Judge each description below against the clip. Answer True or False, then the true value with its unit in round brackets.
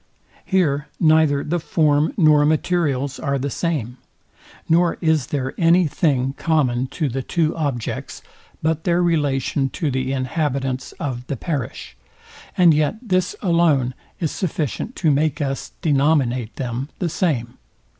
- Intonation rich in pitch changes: False (3.6 semitones)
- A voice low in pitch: False (150 Hz)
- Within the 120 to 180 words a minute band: True (135 wpm)